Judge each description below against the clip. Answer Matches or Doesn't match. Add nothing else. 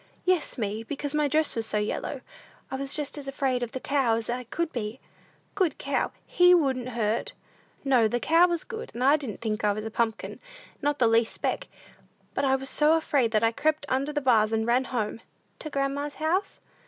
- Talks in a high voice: Matches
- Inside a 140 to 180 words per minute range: Doesn't match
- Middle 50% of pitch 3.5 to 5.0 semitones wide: Matches